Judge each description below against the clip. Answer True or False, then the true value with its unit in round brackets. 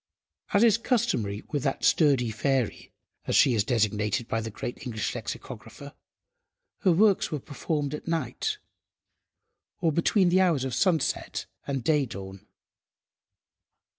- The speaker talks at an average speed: False (130 wpm)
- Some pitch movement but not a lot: False (7.0 semitones)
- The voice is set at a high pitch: False (140 Hz)